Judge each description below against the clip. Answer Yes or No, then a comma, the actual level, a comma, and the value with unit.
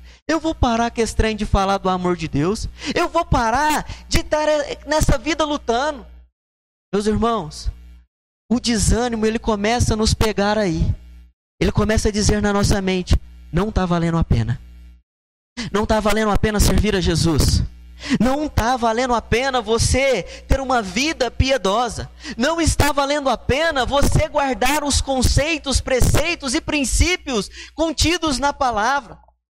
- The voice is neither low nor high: No, high, 230 Hz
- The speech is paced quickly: No, average, 155 wpm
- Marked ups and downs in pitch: Yes, wide, 8.3 semitones